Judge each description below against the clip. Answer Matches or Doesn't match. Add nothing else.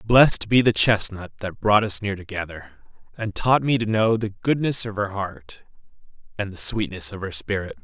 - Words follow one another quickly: Doesn't match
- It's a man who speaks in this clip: Matches